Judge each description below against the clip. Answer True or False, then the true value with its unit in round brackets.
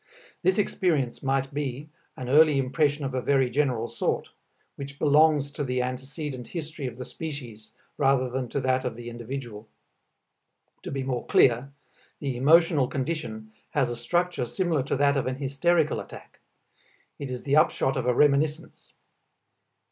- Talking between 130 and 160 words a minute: True (155 wpm)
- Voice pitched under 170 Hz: True (135 Hz)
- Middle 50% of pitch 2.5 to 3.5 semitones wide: True (2.8 semitones)